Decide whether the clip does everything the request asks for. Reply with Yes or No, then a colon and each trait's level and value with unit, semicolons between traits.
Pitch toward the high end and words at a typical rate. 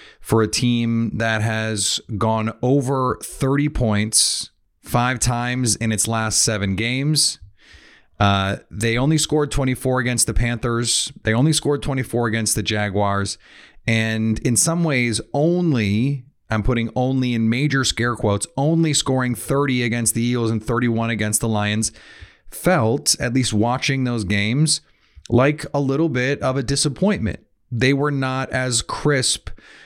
No: low, 120 Hz; average, 145 wpm